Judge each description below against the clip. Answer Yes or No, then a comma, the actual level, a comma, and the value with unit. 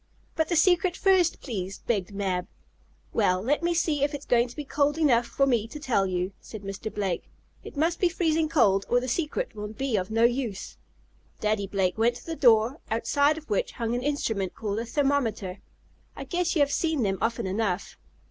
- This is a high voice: Yes, high, 240 Hz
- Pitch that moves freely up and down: Yes, wide, 6.6 semitones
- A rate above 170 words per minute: Yes, fast, 205 wpm